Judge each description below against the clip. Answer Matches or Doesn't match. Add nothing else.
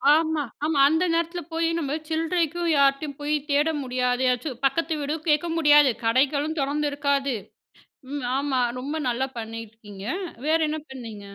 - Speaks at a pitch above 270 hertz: Matches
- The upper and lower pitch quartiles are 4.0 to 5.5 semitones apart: Doesn't match